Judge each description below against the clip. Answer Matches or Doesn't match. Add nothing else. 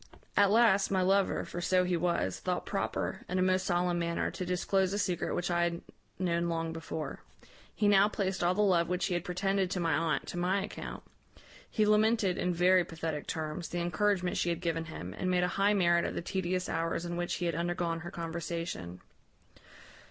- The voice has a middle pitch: Matches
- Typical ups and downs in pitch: Doesn't match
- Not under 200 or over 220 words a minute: Matches